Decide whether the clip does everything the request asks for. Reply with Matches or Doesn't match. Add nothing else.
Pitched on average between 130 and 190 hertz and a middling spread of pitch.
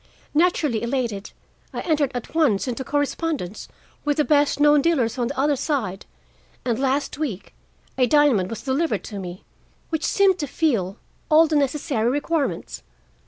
Doesn't match